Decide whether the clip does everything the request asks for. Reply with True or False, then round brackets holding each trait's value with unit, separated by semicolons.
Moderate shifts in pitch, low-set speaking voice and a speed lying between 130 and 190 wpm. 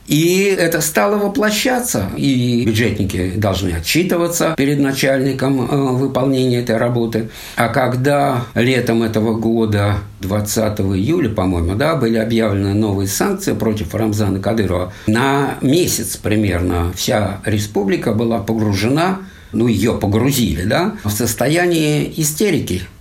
False (4.9 semitones; 115 Hz; 110 wpm)